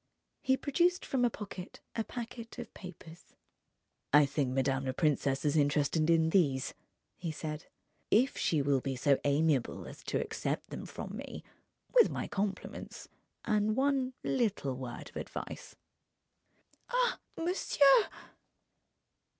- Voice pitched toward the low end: No, medium, 165 Hz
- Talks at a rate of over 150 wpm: No, slow, 135 wpm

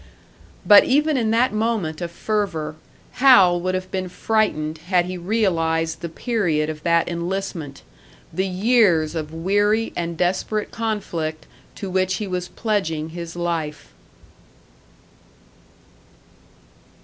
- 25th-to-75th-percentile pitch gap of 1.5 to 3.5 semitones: No, average, 4.4 semitones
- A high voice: No, medium, 180 Hz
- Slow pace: Yes, slow, 120 wpm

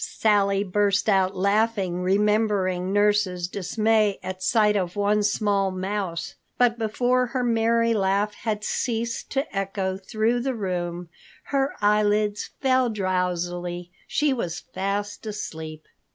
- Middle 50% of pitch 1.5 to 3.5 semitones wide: Yes, average, 2.9 semitones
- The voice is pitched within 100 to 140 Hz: No, high, 205 Hz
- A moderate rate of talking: No, slow, 125 wpm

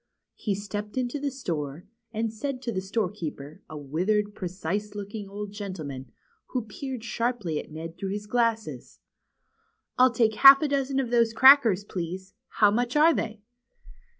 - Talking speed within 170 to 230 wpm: No, average, 160 wpm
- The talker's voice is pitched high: Yes, high, 210 Hz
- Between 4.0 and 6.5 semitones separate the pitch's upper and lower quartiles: Yes, average, 4.5 semitones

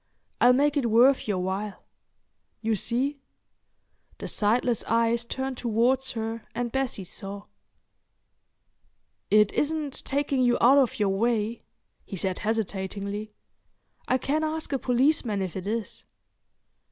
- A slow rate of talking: Yes, slow, 130 wpm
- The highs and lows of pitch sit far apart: No, average, 4.2 semitones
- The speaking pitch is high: Yes, high, 235 Hz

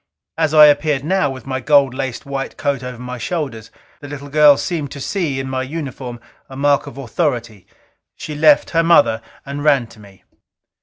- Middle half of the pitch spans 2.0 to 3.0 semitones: Yes, narrow, 2.4 semitones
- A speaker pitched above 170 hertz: No, medium, 140 Hz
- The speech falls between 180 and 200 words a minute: Yes, average, 190 wpm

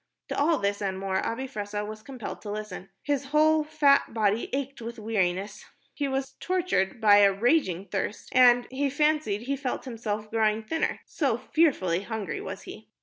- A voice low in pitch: No, high, 225 Hz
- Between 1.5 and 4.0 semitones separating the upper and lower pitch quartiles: No, average, 5.3 semitones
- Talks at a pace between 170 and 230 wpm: Yes, average, 175 wpm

